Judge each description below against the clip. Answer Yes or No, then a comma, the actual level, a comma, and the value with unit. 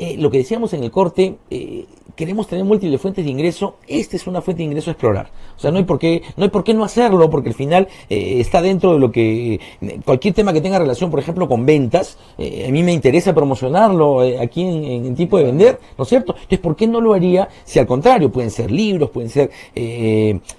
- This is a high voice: No, medium, 170 Hz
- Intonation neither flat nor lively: No, wide, 6.4 semitones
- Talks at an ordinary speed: No, fast, 245 wpm